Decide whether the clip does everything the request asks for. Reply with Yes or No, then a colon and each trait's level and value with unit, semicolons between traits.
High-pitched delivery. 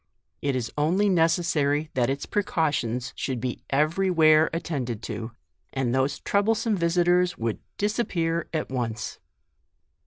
No: medium, 155 Hz